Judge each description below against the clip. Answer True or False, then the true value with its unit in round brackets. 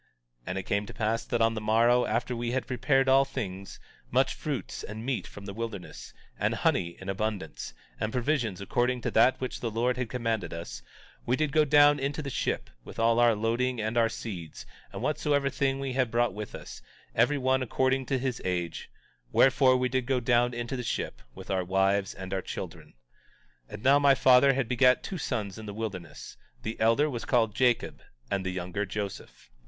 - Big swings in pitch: False (4.1 semitones)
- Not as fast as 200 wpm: False (205 wpm)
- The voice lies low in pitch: True (120 Hz)